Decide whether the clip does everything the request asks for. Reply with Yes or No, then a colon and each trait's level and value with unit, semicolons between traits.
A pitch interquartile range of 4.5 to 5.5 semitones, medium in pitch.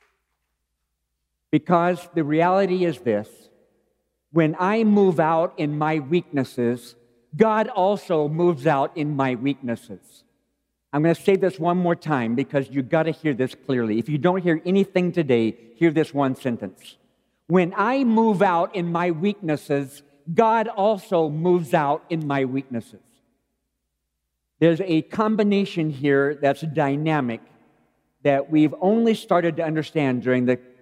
Yes: average, 5.2 semitones; medium, 155 Hz